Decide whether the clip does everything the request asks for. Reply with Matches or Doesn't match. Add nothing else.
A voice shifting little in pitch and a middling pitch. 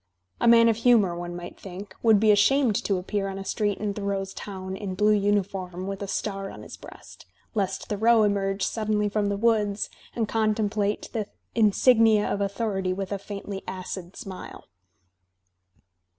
Doesn't match